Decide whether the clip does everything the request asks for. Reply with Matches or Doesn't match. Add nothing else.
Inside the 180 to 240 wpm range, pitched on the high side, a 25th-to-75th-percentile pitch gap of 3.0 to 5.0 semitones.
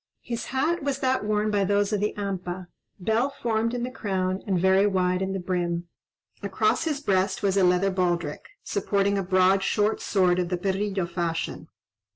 Doesn't match